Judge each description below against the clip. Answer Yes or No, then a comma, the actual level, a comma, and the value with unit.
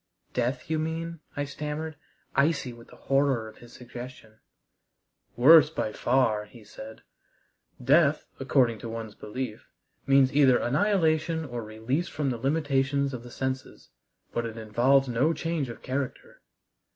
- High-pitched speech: No, low, 130 Hz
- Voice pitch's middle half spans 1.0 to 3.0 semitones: No, average, 4.1 semitones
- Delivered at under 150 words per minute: Yes, average, 140 wpm